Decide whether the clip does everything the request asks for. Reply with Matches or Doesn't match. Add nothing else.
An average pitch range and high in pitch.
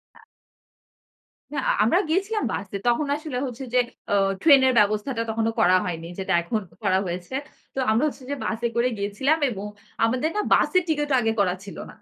Doesn't match